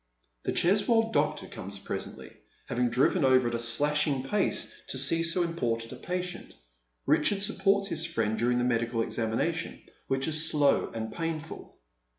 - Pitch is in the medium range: Yes, medium, 145 Hz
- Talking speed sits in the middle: Yes, average, 150 wpm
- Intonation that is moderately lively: No, wide, 6.4 semitones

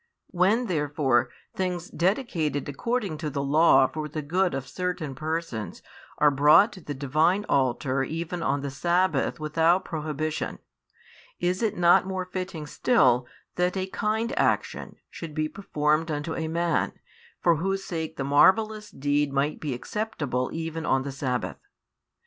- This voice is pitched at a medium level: Yes, medium, 160 Hz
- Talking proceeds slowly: No, average, 150 wpm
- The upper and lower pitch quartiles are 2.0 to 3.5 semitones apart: No, average, 4.1 semitones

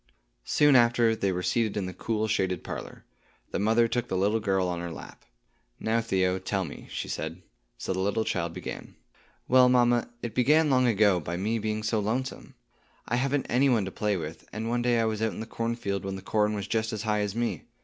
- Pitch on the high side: No, low, 110 Hz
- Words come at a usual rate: No, fast, 220 wpm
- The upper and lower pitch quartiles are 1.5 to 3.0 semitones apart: No, average, 3.6 semitones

